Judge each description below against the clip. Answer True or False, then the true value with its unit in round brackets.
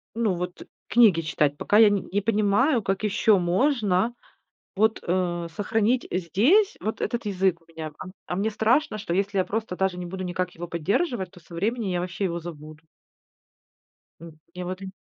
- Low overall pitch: False (190 Hz)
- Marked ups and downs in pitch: False (3.8 semitones)